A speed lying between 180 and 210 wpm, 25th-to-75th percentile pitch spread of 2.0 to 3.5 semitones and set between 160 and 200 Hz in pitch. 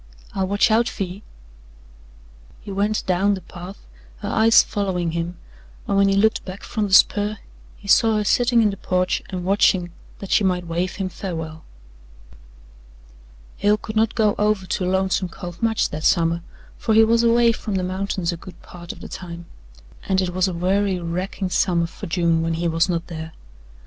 Yes: average, 190 wpm; average, 2.9 semitones; high, 190 Hz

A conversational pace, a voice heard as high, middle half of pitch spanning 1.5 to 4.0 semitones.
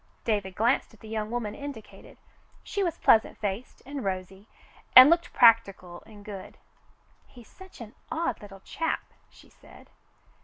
No: average, 150 wpm; high, 220 Hz; average, 4.4 semitones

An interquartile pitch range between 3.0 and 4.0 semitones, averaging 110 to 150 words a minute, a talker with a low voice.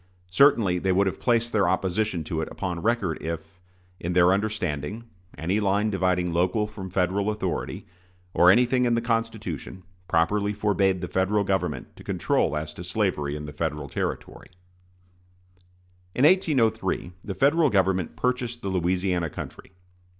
Yes: average, 3.6 semitones; average, 145 wpm; very low, 95 Hz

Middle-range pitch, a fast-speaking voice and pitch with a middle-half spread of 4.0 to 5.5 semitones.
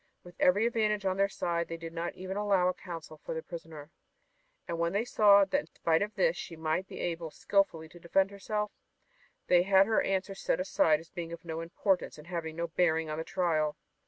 No: medium, 175 Hz; fast, 215 wpm; average, 3.1 semitones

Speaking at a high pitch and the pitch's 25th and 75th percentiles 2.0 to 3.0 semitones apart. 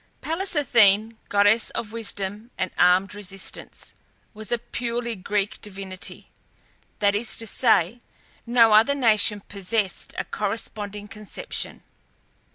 Yes: high, 210 Hz; narrow, 2.5 semitones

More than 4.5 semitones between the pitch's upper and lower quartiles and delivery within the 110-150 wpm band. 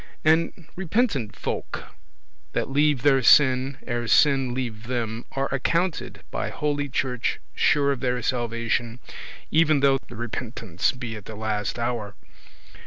No: average, 3.6 semitones; slow, 135 wpm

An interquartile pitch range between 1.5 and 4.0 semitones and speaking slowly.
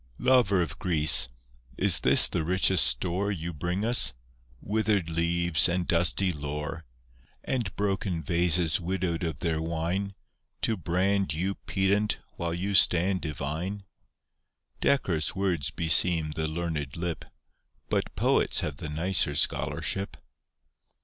Yes: average, 3.2 semitones; slow, 125 wpm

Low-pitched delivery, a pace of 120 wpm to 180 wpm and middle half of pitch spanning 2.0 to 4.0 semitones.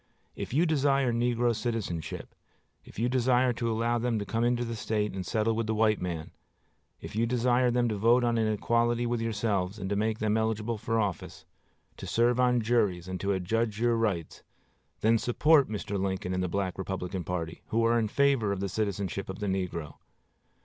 No: low, 110 Hz; average, 200 wpm; average, 3.3 semitones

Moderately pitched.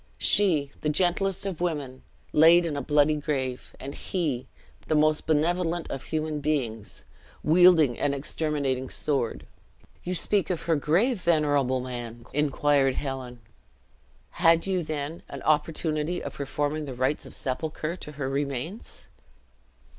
Yes: medium, 150 Hz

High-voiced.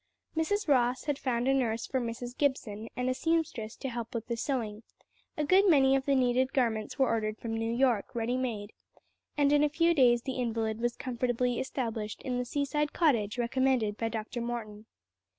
Yes: high, 245 Hz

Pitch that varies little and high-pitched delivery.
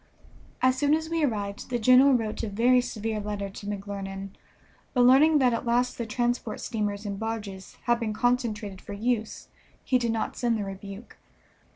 No: average, 3.4 semitones; high, 225 Hz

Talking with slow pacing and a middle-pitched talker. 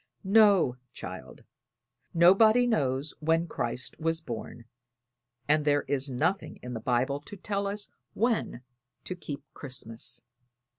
Yes: slow, 120 wpm; medium, 150 Hz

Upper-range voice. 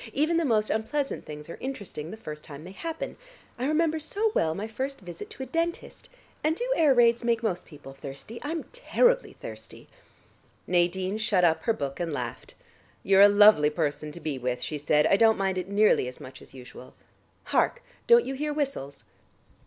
Yes: high, 205 Hz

